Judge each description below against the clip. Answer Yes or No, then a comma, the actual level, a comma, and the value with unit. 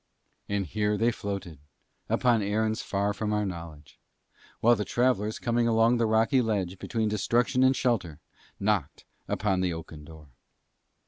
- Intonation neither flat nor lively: Yes, average, 3.6 semitones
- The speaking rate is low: No, average, 145 wpm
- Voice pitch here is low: Yes, low, 105 Hz